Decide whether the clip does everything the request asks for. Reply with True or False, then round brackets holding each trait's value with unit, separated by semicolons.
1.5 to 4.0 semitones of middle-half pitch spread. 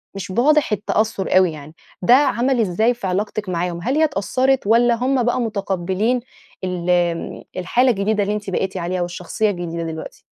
False (5.1 semitones)